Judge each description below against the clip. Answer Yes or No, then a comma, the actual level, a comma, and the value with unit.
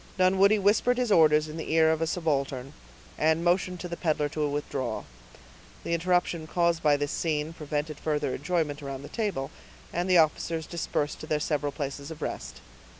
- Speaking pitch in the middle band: Yes, medium, 160 Hz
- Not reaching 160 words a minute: No, average, 180 wpm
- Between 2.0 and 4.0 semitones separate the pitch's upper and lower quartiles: Yes, average, 2.8 semitones